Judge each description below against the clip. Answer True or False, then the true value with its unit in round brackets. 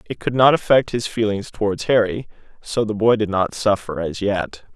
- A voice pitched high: False (105 Hz)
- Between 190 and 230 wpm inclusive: True (200 wpm)